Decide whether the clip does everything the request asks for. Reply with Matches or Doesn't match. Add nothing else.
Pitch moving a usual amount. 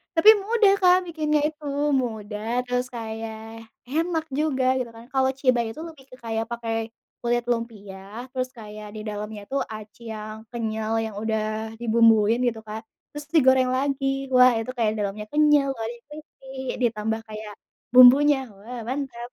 Matches